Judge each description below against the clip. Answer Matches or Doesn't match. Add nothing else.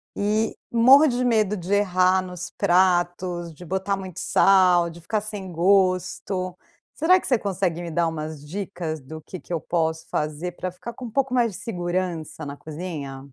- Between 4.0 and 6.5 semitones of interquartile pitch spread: Doesn't match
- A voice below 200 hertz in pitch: Matches